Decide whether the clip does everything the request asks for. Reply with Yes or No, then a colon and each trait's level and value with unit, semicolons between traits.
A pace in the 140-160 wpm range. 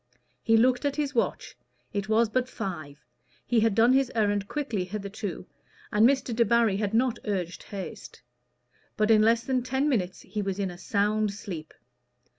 No: average, 170 wpm